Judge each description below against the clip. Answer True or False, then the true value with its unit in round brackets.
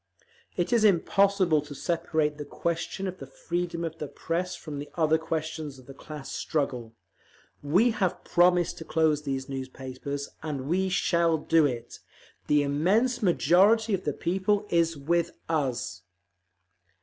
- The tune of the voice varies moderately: True (3.7 semitones)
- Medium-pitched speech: True (160 Hz)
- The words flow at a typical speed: True (150 wpm)